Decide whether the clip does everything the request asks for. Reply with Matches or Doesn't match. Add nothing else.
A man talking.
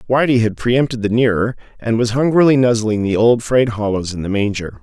Matches